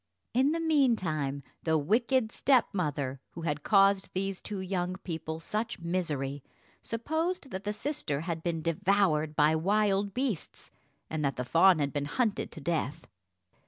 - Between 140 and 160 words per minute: Yes, average, 150 wpm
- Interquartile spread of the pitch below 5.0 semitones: No, wide, 5.6 semitones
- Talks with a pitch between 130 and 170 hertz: No, medium, 180 Hz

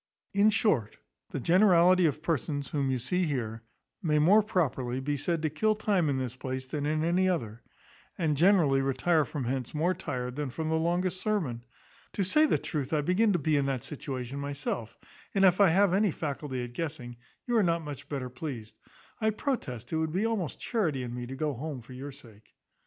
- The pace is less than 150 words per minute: No, fast, 205 wpm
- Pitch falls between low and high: Yes, medium, 150 Hz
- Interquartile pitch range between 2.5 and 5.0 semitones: No, wide, 5.5 semitones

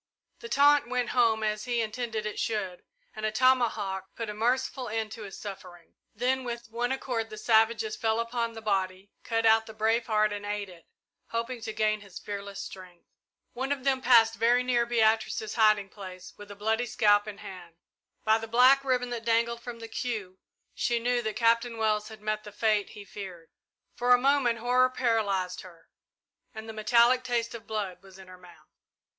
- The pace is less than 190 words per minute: No, average, 195 wpm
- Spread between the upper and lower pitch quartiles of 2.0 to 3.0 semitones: Yes, average, 2.7 semitones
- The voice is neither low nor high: No, high, 225 Hz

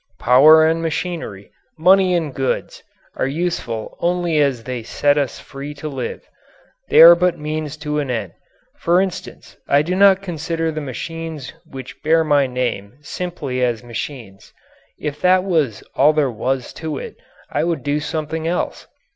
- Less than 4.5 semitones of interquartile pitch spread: Yes, average, 4.0 semitones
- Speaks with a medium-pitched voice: Yes, medium, 150 Hz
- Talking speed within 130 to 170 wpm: Yes, average, 160 wpm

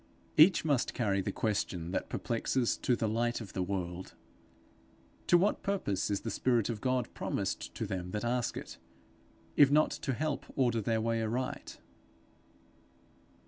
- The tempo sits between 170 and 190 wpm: No, average, 160 wpm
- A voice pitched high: No, low, 115 Hz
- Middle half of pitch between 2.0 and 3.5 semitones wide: No, average, 4.4 semitones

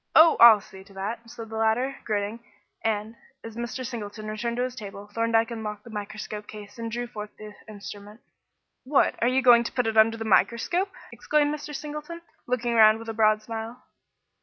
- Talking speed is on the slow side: No, average, 190 wpm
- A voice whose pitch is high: Yes, high, 225 Hz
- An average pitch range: No, narrow, 2.3 semitones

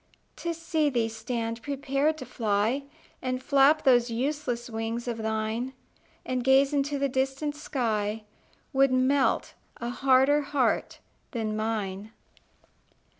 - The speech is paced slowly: Yes, slow, 125 wpm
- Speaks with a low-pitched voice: No, very high, 255 Hz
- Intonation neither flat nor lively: Yes, average, 3.5 semitones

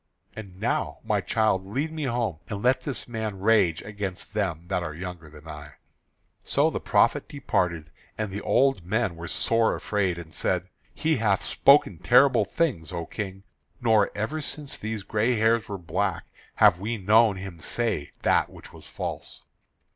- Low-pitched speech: Yes, low, 105 Hz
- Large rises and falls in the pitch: No, average, 4.3 semitones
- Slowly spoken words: No, average, 170 wpm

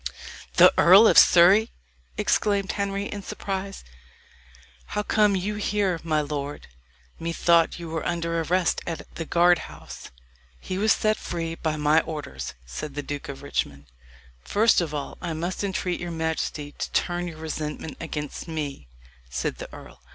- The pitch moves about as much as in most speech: Yes, average, 3.9 semitones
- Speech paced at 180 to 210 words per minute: No, average, 155 wpm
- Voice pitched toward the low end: No, medium, 165 Hz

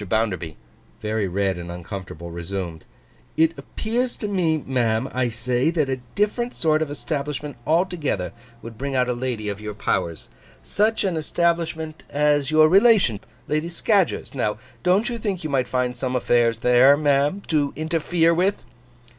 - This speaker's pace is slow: No, average, 155 wpm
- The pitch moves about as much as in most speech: No, wide, 6.7 semitones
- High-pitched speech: No, medium, 140 Hz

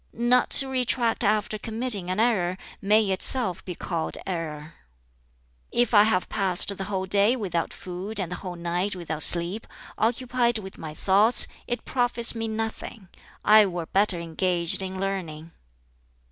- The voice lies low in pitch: No, high, 195 Hz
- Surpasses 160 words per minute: No, average, 150 wpm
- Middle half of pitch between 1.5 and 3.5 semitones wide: No, average, 4.1 semitones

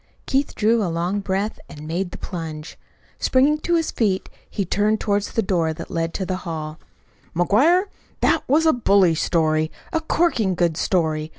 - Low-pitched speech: No, high, 190 Hz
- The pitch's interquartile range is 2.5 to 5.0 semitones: No, wide, 5.4 semitones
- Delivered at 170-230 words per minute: Yes, average, 175 wpm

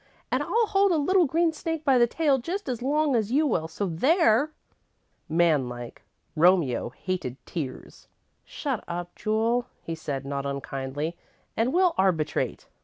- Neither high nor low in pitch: No, high, 220 Hz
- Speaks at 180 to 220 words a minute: No, average, 155 wpm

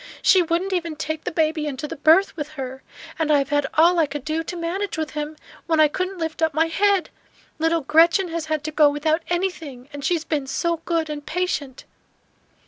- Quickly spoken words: Yes, fast, 220 wpm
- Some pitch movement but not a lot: No, narrow, 2.3 semitones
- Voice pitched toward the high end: Yes, very high, 315 Hz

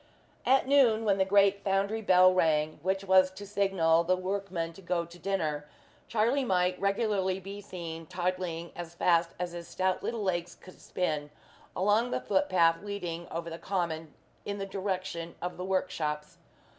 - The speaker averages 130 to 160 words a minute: No, average, 170 wpm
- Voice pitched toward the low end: No, medium, 185 Hz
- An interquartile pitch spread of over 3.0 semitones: No, average, 2.7 semitones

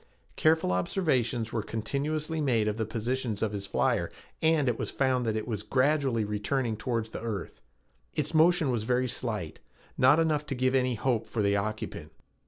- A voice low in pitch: Yes, low, 125 Hz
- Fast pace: No, average, 180 wpm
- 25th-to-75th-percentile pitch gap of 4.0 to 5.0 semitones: Yes, average, 4.3 semitones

